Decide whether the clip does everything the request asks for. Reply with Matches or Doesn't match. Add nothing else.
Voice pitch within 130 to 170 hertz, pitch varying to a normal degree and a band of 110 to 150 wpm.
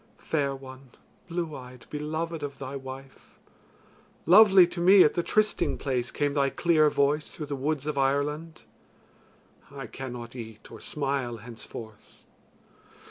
Matches